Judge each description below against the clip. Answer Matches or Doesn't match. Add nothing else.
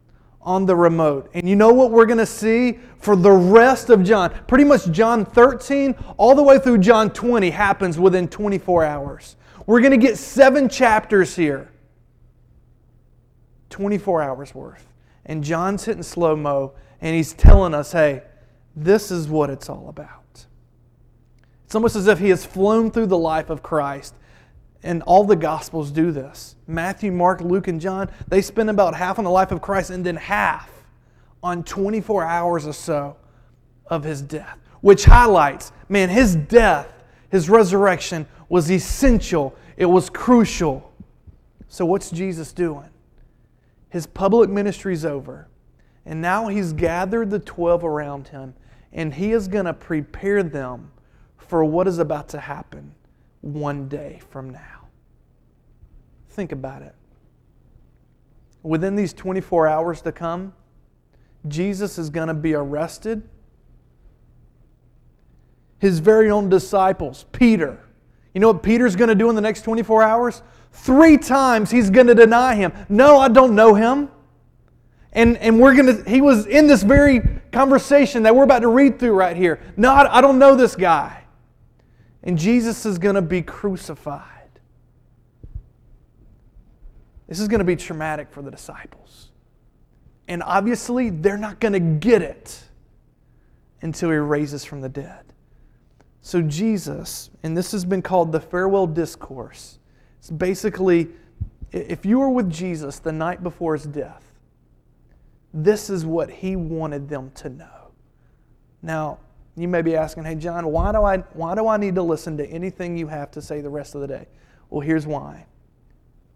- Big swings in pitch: Matches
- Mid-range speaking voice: Matches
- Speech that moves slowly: Doesn't match